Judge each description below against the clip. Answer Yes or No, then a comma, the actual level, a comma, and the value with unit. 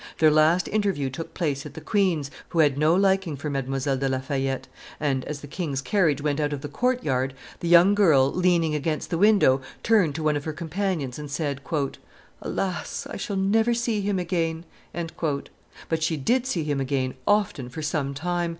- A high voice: No, medium, 155 Hz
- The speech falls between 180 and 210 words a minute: Yes, average, 195 wpm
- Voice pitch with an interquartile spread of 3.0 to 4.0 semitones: No, average, 4.7 semitones